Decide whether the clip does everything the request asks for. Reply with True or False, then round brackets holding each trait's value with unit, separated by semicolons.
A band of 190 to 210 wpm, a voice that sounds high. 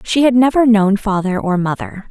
True (200 wpm; 215 Hz)